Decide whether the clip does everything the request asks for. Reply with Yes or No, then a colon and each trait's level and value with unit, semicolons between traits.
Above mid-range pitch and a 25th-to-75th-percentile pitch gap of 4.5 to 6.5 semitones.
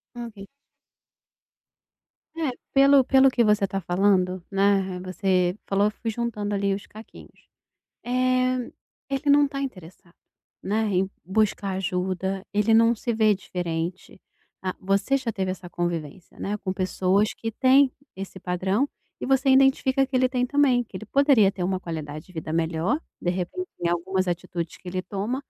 Yes: high, 200 Hz; average, 5.2 semitones